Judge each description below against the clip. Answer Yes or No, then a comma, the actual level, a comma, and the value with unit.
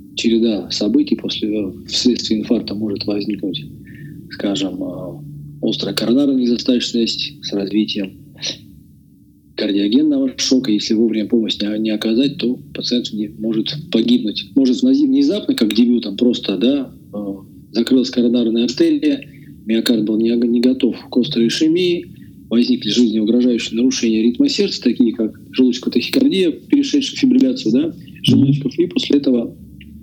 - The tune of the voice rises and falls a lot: Yes, wide, 6.0 semitones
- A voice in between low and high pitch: No, low, 120 Hz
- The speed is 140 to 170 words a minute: No, average, 115 wpm